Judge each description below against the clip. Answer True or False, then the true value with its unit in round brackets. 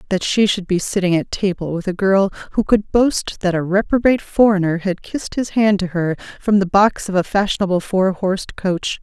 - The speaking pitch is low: False (195 Hz)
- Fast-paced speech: True (215 wpm)